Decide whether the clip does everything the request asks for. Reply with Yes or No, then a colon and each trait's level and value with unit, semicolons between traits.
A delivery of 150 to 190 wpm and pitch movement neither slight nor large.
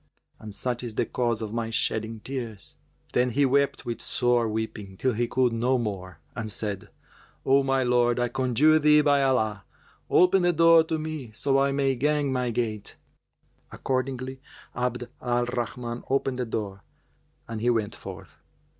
Yes: average, 165 wpm; average, 3.1 semitones